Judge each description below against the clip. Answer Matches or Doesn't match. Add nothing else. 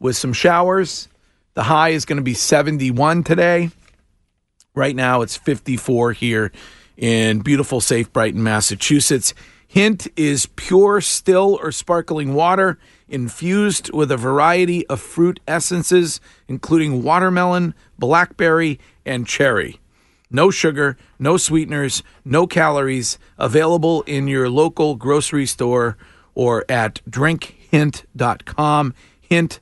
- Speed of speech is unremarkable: Doesn't match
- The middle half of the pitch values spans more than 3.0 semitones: Matches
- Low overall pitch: Doesn't match